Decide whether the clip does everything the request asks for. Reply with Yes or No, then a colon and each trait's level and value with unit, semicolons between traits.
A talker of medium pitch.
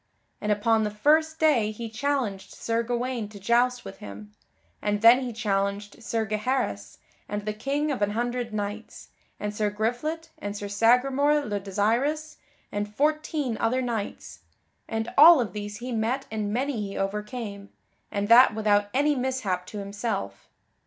No: high, 225 Hz